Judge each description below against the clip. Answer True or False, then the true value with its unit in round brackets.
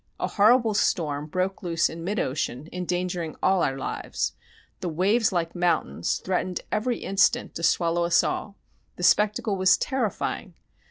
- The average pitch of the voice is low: False (180 Hz)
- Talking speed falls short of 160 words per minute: True (150 wpm)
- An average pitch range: True (3.3 semitones)